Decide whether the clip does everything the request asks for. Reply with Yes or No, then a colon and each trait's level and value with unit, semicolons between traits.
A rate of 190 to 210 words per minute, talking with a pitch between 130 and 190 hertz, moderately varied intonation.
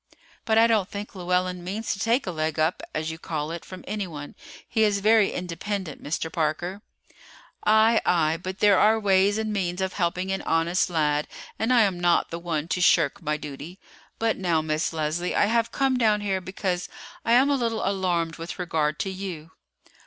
Yes: average, 195 wpm; medium, 185 Hz; average, 4.2 semitones